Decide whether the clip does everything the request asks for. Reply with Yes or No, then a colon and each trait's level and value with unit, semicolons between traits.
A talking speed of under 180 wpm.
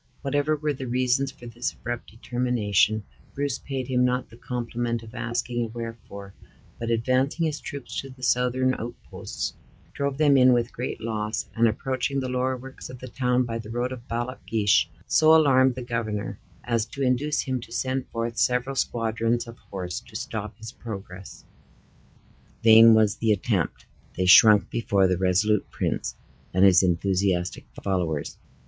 Yes: average, 165 wpm